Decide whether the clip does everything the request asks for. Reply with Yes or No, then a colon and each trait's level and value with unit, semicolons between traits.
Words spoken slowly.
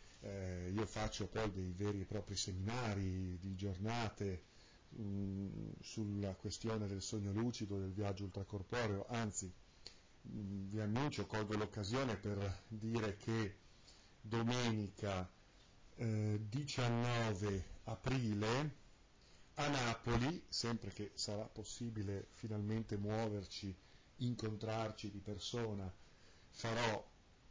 Yes: slow, 100 wpm